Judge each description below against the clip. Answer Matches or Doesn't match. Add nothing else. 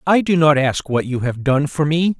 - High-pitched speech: Doesn't match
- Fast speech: Matches